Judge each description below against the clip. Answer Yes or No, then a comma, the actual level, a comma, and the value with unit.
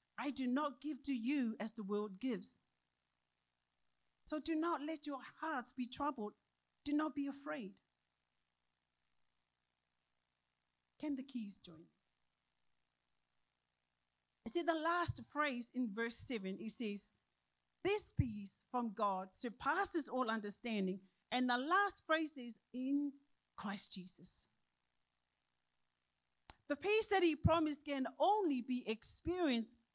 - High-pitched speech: Yes, high, 220 Hz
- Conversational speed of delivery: No, slow, 120 wpm